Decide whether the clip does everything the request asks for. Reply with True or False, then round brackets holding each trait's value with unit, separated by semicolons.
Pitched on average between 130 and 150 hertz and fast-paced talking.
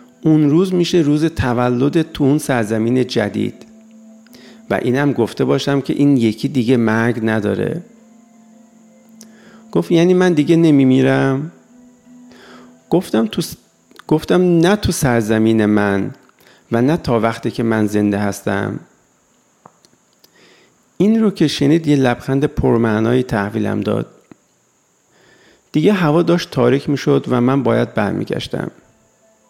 False (140 Hz; 115 wpm)